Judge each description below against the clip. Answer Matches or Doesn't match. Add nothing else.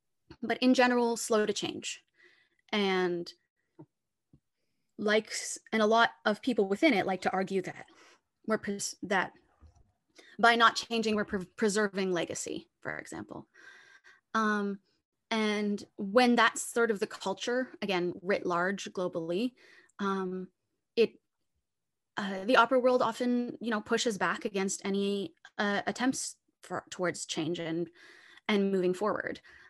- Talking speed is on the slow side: Matches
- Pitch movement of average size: Matches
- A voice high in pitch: Matches